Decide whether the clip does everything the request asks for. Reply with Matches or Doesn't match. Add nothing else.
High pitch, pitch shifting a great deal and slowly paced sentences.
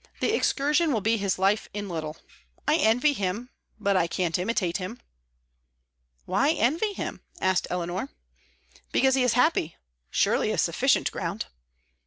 Doesn't match